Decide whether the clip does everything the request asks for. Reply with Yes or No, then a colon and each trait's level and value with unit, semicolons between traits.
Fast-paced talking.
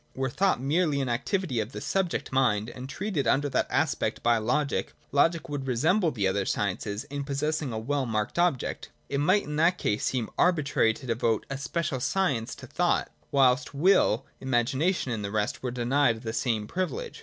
No: average, 185 wpm